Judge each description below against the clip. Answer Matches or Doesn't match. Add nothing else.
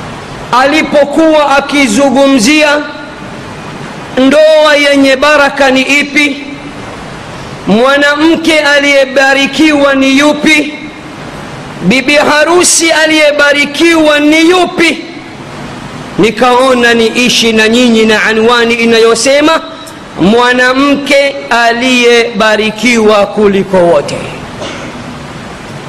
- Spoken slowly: Matches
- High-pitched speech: Matches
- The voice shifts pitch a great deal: Doesn't match